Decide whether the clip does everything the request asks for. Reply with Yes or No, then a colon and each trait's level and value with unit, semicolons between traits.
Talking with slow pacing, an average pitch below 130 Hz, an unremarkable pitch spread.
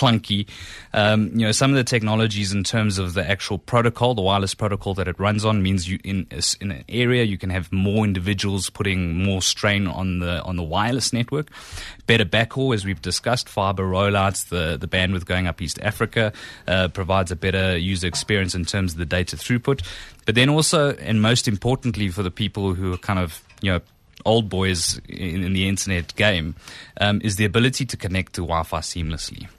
No: average, 200 wpm; low, 100 Hz; average, 3.1 semitones